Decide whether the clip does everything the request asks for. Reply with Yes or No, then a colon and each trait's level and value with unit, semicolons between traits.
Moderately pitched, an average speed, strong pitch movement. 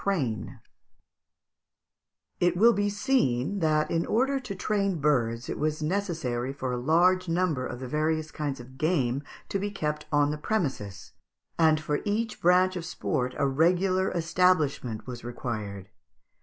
Yes: medium, 155 Hz; average, 150 wpm; wide, 6.1 semitones